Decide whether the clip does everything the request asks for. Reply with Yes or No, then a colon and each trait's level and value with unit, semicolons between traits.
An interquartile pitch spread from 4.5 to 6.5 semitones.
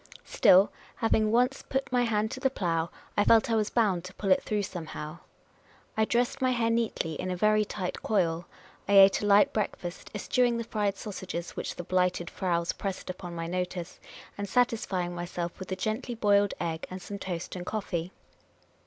No: average, 3.7 semitones